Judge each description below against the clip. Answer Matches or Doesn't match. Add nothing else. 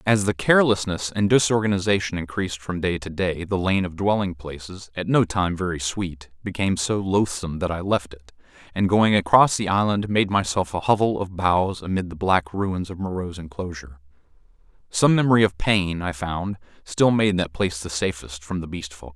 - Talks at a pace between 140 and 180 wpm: Doesn't match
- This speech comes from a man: Matches